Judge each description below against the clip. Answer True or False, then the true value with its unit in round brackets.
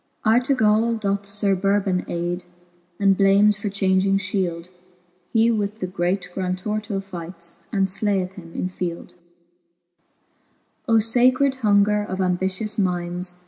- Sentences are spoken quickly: False (135 wpm)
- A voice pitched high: True (195 Hz)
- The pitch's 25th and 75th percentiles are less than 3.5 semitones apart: True (2.4 semitones)